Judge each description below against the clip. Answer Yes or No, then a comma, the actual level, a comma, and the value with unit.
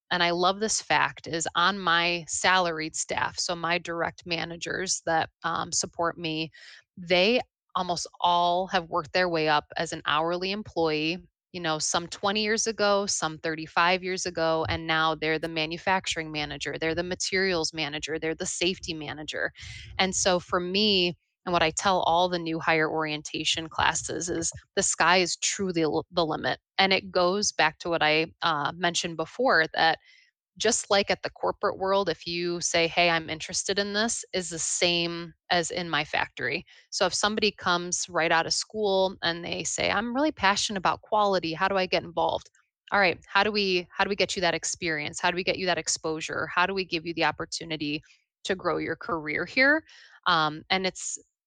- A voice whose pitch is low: No, medium, 175 Hz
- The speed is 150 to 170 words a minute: No, average, 190 wpm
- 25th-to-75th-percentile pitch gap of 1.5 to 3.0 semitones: Yes, narrow, 2.6 semitones